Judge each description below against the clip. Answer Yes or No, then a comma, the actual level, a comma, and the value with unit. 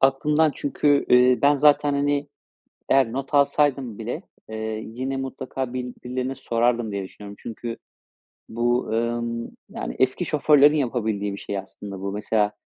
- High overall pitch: No, low, 125 Hz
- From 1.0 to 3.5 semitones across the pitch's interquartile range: No, average, 4.0 semitones